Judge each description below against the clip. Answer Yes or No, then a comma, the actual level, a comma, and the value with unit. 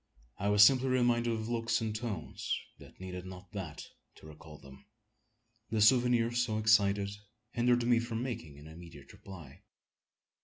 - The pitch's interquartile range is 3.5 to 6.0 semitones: Yes, average, 4.6 semitones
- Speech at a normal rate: Yes, average, 150 wpm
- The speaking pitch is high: No, low, 110 Hz